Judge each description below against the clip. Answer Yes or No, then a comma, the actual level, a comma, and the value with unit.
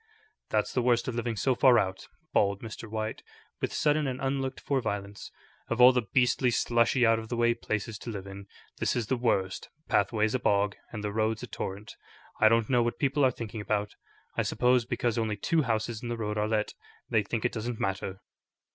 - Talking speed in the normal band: No, fast, 210 wpm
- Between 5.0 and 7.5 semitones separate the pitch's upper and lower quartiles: No, narrow, 2.6 semitones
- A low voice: Yes, low, 115 Hz